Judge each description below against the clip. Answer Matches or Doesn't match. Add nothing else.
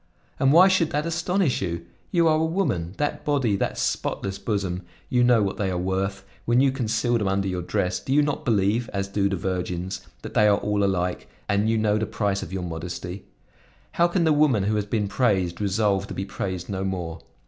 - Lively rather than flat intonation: Doesn't match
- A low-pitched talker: Matches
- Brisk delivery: Matches